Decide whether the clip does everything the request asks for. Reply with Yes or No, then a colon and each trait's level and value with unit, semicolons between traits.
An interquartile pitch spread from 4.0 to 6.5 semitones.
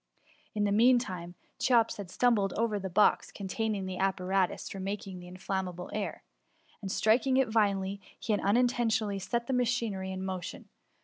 No: average, 3.2 semitones